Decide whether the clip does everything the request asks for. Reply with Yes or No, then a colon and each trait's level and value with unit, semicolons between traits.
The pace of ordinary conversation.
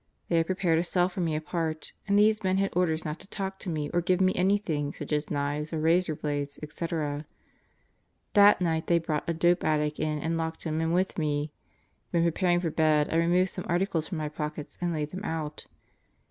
No: fast, 215 wpm